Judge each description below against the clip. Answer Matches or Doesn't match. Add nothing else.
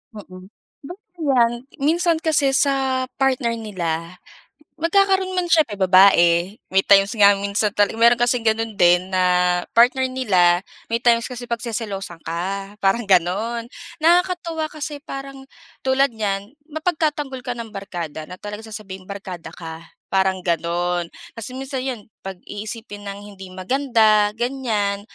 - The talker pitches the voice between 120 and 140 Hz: Doesn't match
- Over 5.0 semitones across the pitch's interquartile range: Matches